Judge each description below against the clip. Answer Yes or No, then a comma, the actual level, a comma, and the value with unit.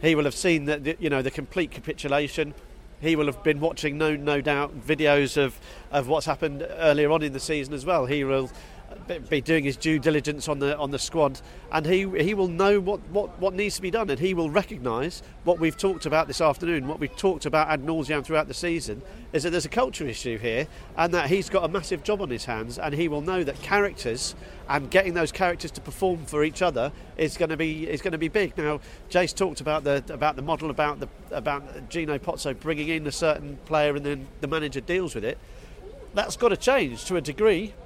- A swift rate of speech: Yes, fast, 230 wpm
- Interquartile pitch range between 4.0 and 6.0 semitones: No, average, 3.3 semitones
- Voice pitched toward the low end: No, medium, 155 Hz